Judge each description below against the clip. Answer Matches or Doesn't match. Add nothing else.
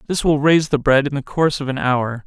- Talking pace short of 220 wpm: Doesn't match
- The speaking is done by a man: Matches